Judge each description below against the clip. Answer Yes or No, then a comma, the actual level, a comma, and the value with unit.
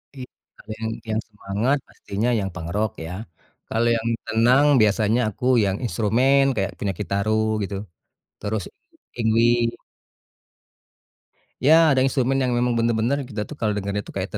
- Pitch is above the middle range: No, low, 110 Hz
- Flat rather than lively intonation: No, average, 3.1 semitones